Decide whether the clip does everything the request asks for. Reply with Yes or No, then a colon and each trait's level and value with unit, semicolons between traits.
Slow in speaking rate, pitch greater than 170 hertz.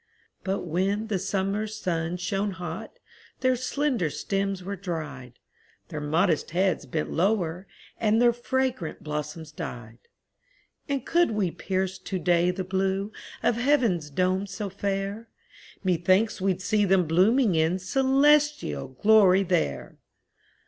Yes: slow, 130 wpm; high, 190 Hz